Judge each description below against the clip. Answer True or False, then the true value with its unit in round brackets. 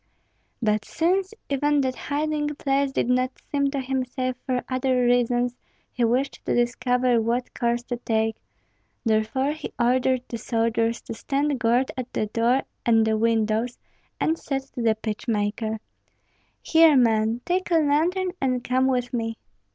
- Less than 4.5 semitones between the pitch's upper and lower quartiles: True (3.0 semitones)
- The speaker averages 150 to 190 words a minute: True (160 wpm)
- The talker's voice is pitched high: True (250 Hz)